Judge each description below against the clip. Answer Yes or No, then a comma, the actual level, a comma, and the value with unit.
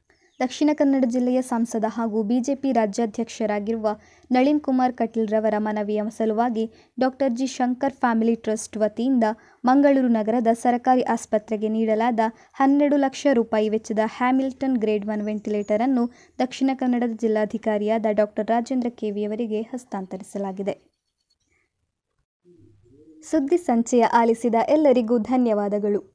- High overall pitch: Yes, high, 230 Hz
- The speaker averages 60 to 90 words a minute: No, fast, 105 wpm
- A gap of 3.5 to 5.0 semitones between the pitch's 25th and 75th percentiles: No, average, 2.9 semitones